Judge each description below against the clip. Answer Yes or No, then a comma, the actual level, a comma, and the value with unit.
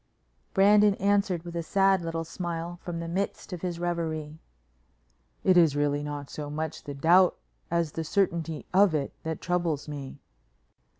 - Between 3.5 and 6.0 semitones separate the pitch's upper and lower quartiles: No, average, 2.8 semitones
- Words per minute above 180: No, average, 160 wpm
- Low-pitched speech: No, medium, 170 Hz